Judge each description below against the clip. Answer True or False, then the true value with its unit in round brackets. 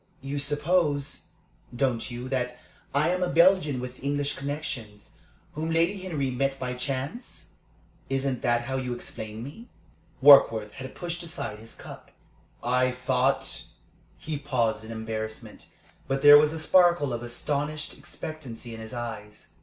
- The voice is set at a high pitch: False (135 Hz)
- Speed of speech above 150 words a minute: False (145 wpm)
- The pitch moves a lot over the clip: False (3.8 semitones)